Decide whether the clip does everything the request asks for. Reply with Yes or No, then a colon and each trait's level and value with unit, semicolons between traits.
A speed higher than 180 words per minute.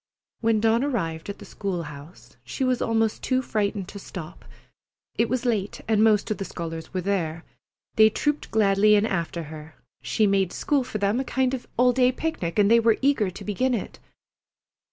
Yes: average, 195 wpm